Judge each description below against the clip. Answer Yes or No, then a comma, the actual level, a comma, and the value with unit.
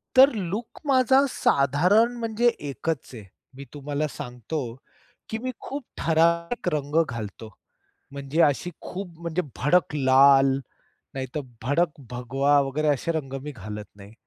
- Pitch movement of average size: Yes, average, 4.8 semitones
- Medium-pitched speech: Yes, medium, 150 Hz